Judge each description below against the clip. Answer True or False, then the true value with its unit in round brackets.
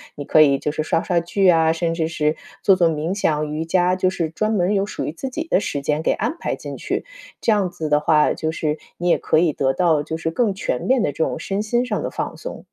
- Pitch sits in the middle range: True (165 Hz)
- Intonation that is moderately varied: True (4.0 semitones)